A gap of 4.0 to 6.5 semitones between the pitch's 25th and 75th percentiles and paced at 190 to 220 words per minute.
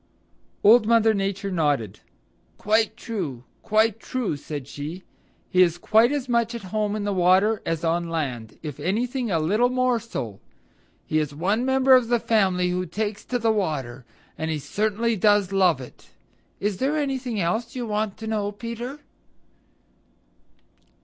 No: average, 5.2 semitones; average, 155 wpm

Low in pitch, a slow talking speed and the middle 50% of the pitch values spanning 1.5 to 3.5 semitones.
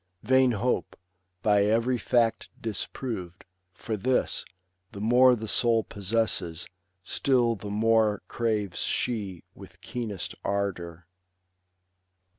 Yes: low, 110 Hz; slow, 100 wpm; average, 2.9 semitones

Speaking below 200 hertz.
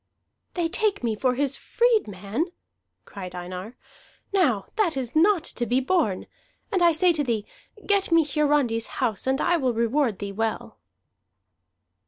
No: very high, 265 Hz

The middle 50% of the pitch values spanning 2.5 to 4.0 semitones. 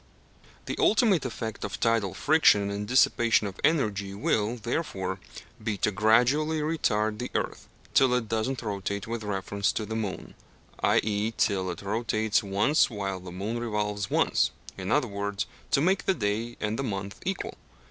Yes: average, 3.2 semitones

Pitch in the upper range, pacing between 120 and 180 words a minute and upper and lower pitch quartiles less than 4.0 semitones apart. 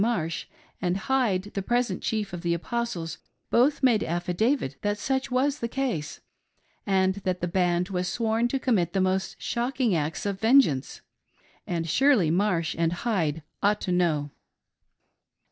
No: high, 195 Hz; average, 155 wpm; wide, 5.5 semitones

